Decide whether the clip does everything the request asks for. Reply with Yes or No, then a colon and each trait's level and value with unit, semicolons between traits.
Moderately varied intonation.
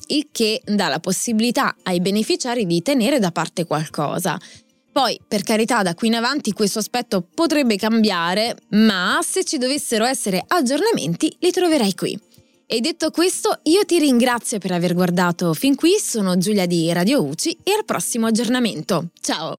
No: wide, 7.3 semitones